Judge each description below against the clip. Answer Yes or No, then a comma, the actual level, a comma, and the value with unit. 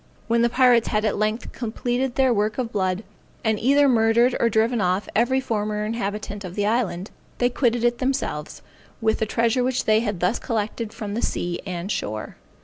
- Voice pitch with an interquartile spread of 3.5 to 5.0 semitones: No, average, 2.7 semitones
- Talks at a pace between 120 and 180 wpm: No, average, 190 wpm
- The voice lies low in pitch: No, high, 225 Hz